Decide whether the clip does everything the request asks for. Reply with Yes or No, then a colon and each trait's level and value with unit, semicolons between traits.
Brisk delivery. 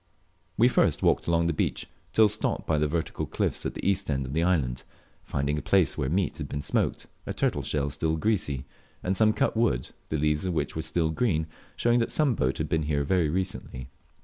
Yes: fast, 220 wpm